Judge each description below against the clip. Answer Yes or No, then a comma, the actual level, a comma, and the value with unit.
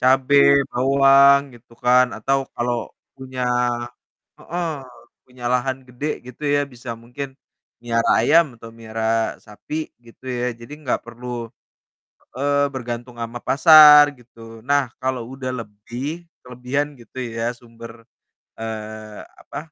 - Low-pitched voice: Yes, low, 125 Hz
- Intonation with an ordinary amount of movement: Yes, average, 3.0 semitones